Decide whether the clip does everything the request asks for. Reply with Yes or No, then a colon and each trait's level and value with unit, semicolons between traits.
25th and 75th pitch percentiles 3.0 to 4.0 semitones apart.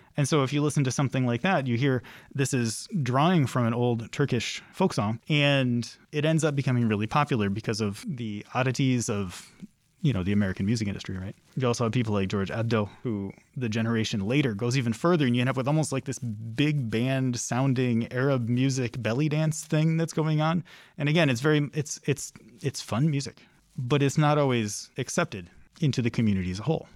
No: average, 4.5 semitones